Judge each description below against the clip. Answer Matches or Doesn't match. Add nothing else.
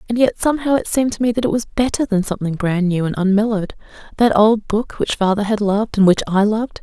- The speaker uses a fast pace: Matches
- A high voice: Matches